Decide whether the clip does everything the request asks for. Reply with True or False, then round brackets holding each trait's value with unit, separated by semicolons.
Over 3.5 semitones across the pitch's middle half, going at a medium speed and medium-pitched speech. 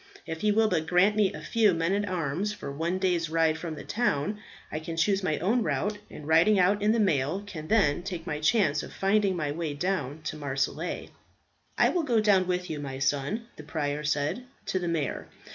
False (5.1 semitones; 210 wpm; 170 Hz)